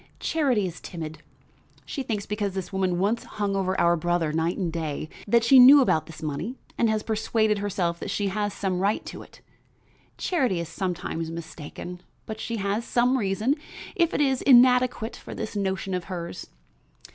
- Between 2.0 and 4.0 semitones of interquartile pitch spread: No, average, 4.9 semitones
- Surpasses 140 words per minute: Yes, average, 180 wpm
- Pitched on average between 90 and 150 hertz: No, high, 200 Hz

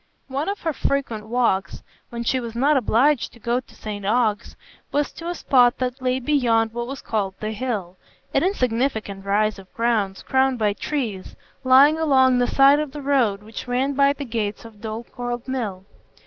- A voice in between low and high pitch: No, high, 245 Hz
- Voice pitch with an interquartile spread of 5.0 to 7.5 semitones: No, average, 4.0 semitones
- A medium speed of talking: Yes, average, 180 wpm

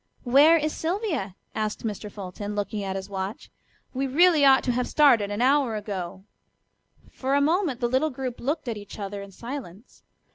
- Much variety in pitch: Yes, wide, 5.7 semitones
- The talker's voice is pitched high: Yes, high, 240 Hz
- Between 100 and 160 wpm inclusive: No, average, 180 wpm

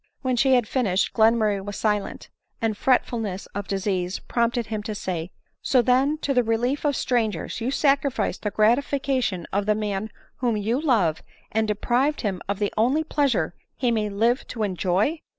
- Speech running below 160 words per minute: No, average, 175 wpm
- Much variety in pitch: No, average, 3.8 semitones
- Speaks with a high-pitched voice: Yes, high, 220 Hz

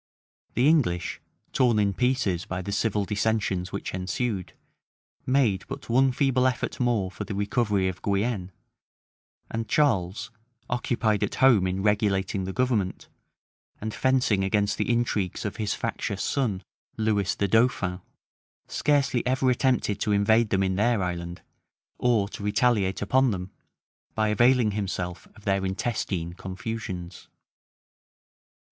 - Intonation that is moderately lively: Yes, average, 4.2 semitones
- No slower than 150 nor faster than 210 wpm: No, slow, 135 wpm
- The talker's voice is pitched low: Yes, low, 105 Hz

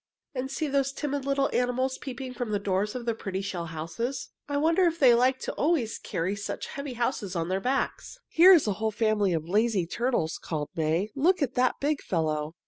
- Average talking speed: No, fast, 215 wpm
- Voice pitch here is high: Yes, high, 235 Hz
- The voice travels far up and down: Yes, wide, 6.1 semitones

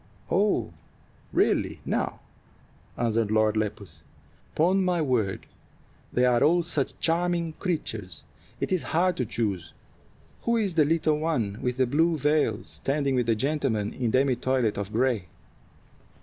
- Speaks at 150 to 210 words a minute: No, average, 140 wpm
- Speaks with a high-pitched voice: No, low, 130 Hz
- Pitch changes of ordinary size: No, wide, 6.7 semitones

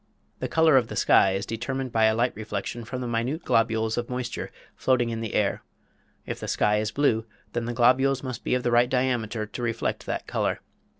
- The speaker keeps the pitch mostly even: Yes, narrow, 2.3 semitones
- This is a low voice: Yes, low, 120 Hz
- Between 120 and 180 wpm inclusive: No, fast, 205 wpm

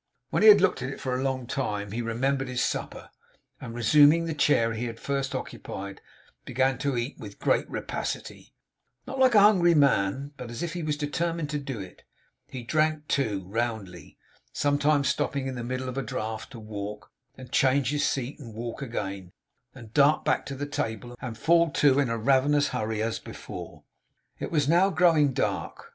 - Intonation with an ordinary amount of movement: Yes, average, 4.3 semitones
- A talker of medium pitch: No, low, 130 Hz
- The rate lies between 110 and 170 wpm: No, average, 190 wpm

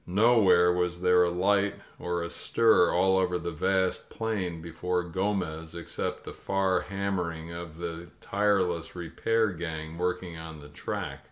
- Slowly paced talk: No, average, 150 wpm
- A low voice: Yes, very low, 90 Hz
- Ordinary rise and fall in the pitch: No, narrow, 2.3 semitones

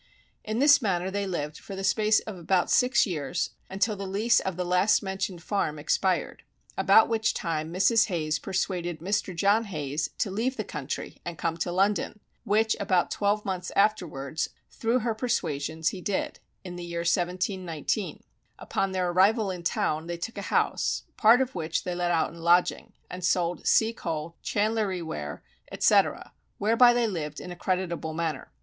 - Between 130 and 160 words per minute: No, average, 175 wpm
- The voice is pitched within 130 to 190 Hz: Yes, medium, 185 Hz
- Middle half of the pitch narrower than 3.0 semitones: No, average, 3.8 semitones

